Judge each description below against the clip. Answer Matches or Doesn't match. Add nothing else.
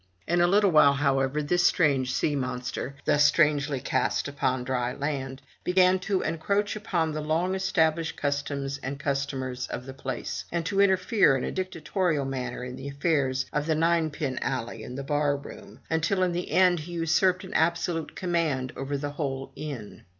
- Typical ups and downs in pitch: Matches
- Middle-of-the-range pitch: Matches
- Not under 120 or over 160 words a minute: Doesn't match